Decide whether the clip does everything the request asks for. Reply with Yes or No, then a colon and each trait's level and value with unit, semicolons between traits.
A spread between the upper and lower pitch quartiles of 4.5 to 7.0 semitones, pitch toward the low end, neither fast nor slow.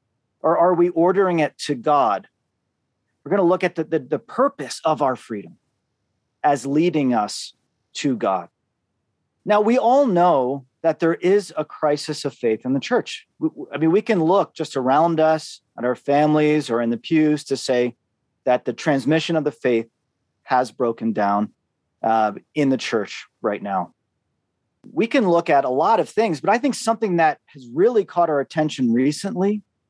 No: average, 5.2 semitones; medium, 150 Hz; average, 180 wpm